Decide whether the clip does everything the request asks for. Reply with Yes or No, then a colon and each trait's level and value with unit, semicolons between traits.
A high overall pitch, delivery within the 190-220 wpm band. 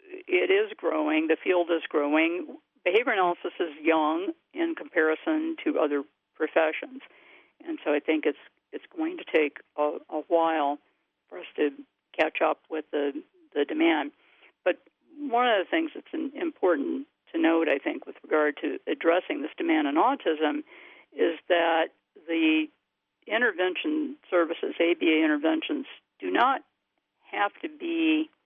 No: very high, 280 Hz; average, 145 wpm